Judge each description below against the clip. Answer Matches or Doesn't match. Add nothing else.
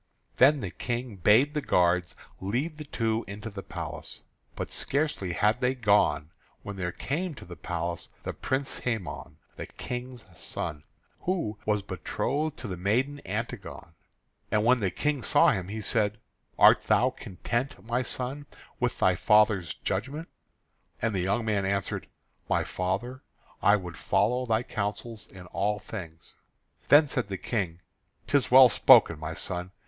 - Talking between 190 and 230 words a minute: Doesn't match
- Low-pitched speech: Matches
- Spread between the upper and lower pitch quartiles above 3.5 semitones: Matches